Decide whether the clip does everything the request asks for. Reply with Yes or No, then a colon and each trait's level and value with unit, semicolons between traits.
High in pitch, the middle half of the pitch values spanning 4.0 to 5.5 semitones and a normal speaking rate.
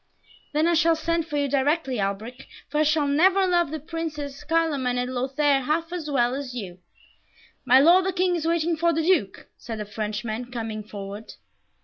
Yes: very high, 285 Hz; average, 5.1 semitones; average, 190 wpm